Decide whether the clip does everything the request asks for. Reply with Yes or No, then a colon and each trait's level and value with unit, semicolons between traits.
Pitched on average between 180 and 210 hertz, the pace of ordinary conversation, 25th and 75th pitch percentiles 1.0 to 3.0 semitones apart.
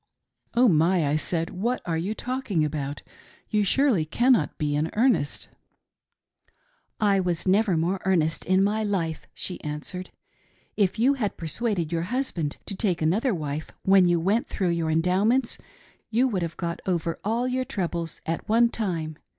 No: medium, 185 Hz; average, 170 wpm; average, 5.2 semitones